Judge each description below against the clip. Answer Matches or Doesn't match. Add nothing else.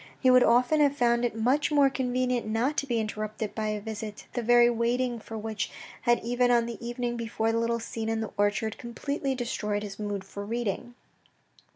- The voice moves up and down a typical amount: Doesn't match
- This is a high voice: Matches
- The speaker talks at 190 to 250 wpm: Matches